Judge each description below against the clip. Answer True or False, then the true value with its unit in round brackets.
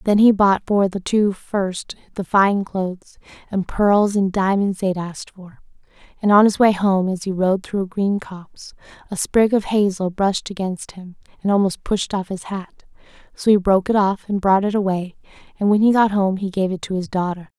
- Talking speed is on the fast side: True (215 wpm)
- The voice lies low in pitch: False (195 Hz)